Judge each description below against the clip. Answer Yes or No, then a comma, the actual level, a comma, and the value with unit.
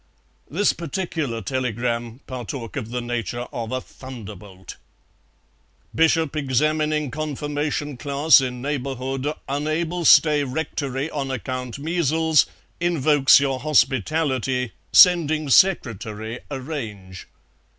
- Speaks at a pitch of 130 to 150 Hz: Yes, low, 135 Hz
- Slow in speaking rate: Yes, slow, 95 wpm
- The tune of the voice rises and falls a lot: No, average, 3.7 semitones